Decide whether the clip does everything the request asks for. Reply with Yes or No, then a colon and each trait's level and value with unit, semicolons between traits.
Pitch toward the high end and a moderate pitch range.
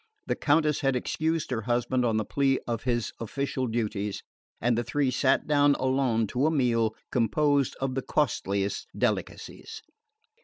No: low, 130 Hz; average, 3.6 semitones